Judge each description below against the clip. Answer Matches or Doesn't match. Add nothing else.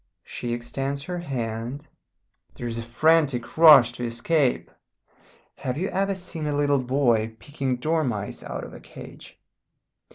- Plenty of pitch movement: Doesn't match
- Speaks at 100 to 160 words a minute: Matches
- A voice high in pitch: Doesn't match